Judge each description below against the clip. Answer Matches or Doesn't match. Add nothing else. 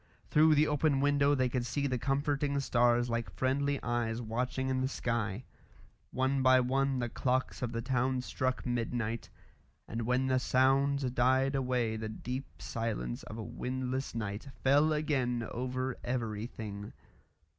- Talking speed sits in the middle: Matches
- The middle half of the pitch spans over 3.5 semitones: Doesn't match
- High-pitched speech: Doesn't match